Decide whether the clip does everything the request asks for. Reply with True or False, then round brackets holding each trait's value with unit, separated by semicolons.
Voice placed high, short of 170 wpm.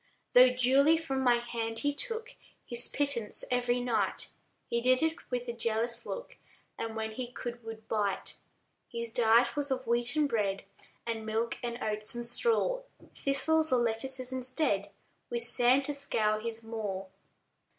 True (240 Hz; 155 wpm)